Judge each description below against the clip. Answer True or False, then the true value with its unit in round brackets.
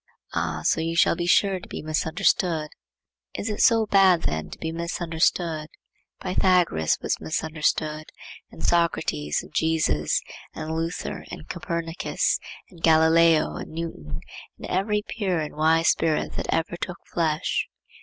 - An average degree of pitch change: False (2.1 semitones)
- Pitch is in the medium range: True (165 Hz)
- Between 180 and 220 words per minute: False (135 wpm)